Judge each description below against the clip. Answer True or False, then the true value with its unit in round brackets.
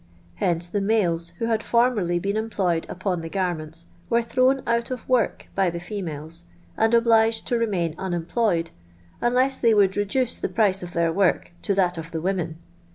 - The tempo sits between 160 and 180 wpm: True (175 wpm)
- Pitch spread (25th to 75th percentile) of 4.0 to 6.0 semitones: True (4.9 semitones)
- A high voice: True (195 Hz)